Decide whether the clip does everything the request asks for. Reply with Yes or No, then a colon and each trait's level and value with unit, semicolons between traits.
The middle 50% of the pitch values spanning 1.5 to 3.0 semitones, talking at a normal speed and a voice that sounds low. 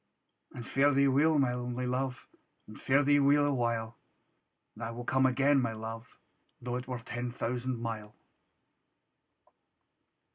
Yes: narrow, 2.5 semitones; average, 150 wpm; low, 125 Hz